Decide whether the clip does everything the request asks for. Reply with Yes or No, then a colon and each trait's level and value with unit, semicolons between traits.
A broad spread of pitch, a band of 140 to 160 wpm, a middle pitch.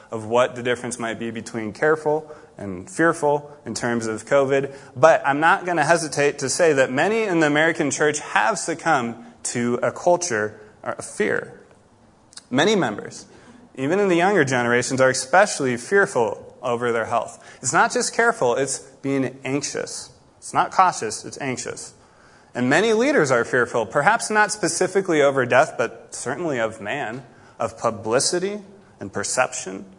Yes: wide, 6.3 semitones; average, 155 wpm; medium, 145 Hz